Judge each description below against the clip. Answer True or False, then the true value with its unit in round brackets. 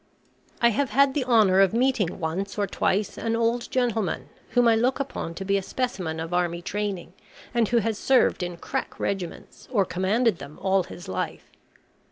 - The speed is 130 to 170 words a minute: False (185 wpm)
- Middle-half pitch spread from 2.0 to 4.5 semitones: False (4.9 semitones)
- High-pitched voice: True (205 Hz)